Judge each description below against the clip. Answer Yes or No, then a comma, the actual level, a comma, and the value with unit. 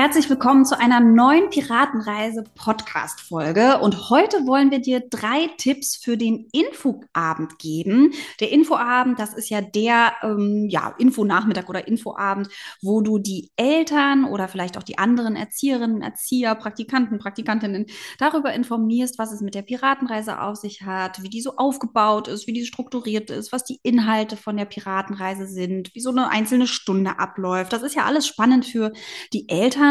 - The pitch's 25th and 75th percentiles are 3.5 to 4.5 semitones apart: Yes, average, 3.8 semitones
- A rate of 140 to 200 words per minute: Yes, average, 170 wpm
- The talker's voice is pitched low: No, high, 225 Hz